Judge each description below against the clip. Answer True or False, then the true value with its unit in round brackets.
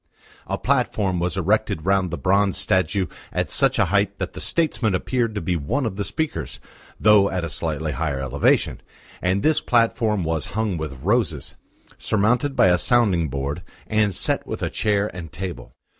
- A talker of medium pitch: False (95 Hz)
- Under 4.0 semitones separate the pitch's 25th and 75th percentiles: False (4.5 semitones)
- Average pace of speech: True (175 wpm)